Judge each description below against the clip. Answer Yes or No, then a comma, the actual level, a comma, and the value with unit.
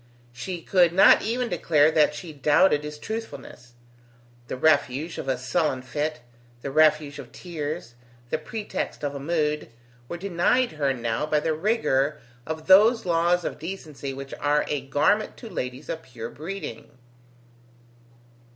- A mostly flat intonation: No, average, 4.1 semitones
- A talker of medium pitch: Yes, medium, 155 Hz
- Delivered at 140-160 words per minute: Yes, average, 150 wpm